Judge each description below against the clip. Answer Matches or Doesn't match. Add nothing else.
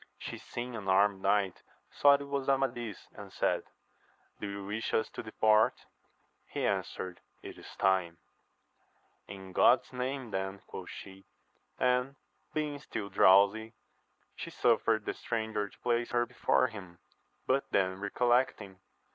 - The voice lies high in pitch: Doesn't match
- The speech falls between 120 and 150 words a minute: Matches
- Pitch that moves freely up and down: Doesn't match